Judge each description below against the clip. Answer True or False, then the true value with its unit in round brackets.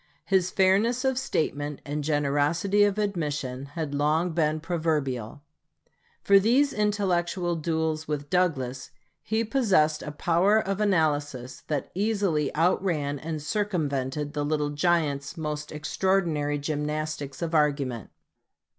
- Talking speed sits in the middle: False (120 wpm)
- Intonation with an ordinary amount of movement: True (4.4 semitones)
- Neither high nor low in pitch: True (155 Hz)